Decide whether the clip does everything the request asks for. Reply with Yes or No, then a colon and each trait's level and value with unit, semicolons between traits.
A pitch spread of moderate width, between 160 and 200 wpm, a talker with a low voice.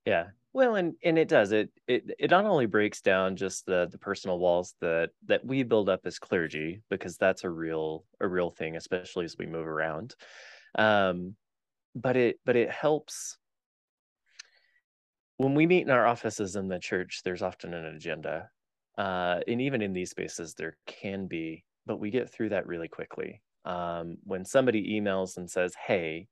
Yes: average, 4.4 semitones; average, 180 wpm; very low, 95 Hz